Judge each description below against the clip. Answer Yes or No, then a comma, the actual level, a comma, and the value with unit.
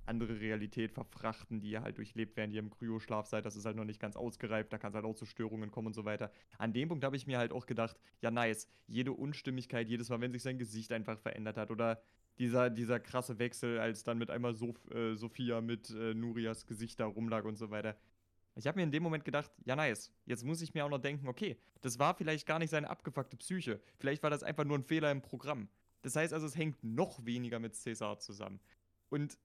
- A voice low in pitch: Yes, low, 115 Hz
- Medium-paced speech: No, fast, 240 wpm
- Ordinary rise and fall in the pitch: Yes, average, 3.4 semitones